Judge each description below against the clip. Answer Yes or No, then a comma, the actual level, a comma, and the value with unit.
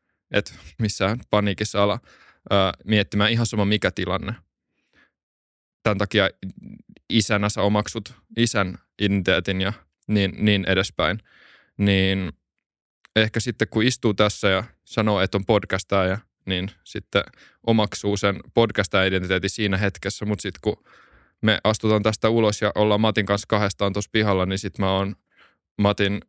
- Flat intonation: Yes, narrow, 2.0 semitones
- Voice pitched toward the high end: No, low, 100 Hz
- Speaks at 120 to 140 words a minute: Yes, average, 135 wpm